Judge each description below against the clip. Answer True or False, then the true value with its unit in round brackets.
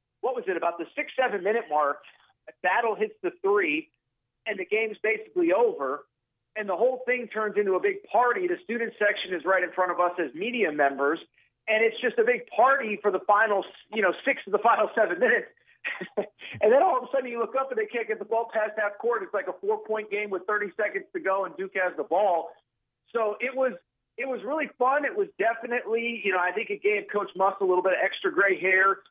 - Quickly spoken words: True (240 wpm)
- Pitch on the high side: True (225 Hz)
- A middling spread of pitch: False (7.6 semitones)